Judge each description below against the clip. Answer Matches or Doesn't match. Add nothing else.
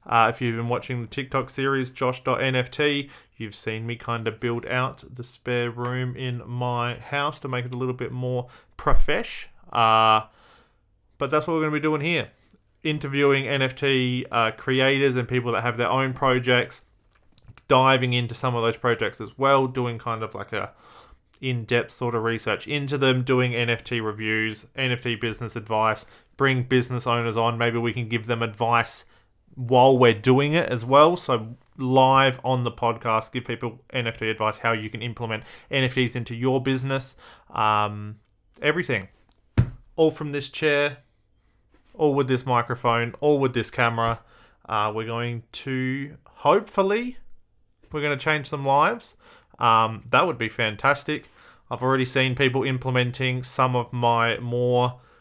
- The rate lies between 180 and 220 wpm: Doesn't match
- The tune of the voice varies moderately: Doesn't match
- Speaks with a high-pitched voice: Doesn't match